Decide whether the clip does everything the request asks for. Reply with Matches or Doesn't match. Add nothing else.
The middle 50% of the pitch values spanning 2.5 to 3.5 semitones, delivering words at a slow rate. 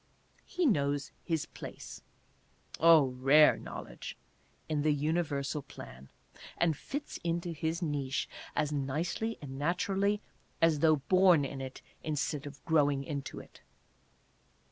Matches